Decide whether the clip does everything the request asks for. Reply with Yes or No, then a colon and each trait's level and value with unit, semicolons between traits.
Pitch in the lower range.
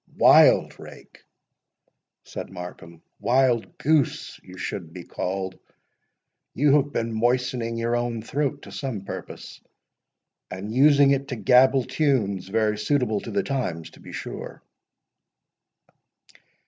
Yes: low, 115 Hz